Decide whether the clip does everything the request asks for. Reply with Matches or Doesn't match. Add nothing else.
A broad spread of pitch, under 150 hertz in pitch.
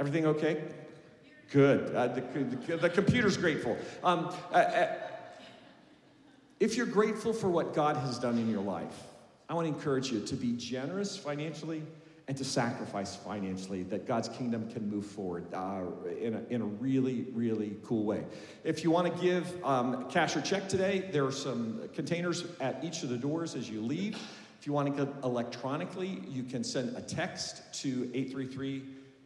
Matches